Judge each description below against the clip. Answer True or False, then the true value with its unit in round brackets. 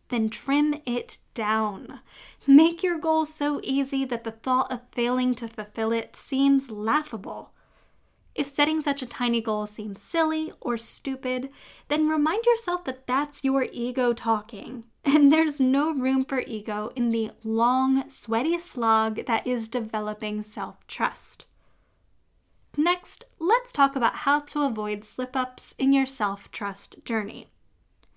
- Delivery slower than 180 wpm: True (145 wpm)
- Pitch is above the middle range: True (255 Hz)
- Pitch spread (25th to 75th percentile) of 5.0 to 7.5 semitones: False (4.3 semitones)